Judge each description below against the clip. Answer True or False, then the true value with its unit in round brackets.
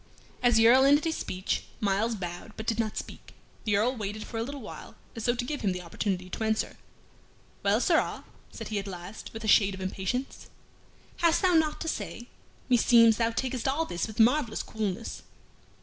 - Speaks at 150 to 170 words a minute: False (195 wpm)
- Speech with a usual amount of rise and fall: True (3.9 semitones)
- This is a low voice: False (225 Hz)